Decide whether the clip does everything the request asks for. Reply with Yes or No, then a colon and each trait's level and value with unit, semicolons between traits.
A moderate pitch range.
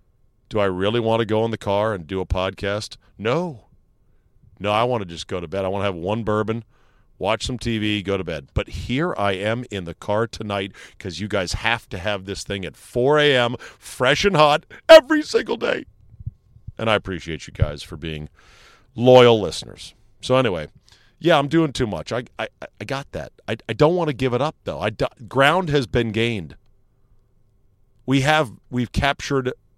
Yes: average, 4.1 semitones